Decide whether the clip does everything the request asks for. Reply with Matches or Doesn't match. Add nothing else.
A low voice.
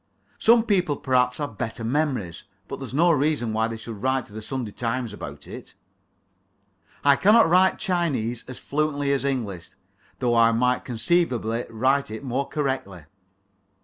Matches